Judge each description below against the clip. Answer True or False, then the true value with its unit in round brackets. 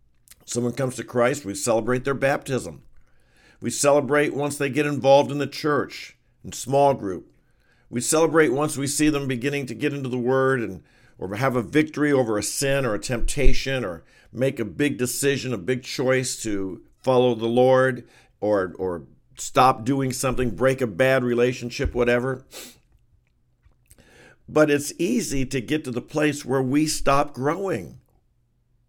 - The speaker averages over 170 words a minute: False (160 wpm)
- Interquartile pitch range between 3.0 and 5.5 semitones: False (2.6 semitones)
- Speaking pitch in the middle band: False (130 Hz)